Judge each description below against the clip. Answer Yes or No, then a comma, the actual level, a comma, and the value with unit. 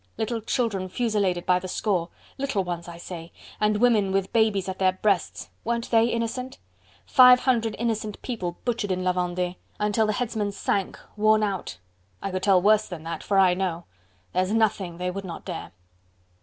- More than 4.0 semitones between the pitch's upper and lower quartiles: No, average, 3.5 semitones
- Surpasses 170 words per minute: Yes, average, 180 wpm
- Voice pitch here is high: Yes, high, 200 Hz